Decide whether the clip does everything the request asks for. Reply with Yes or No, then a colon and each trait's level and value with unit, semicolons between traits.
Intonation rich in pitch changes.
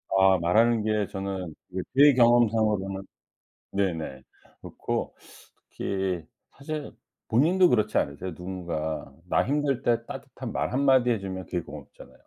No: average, 4.7 semitones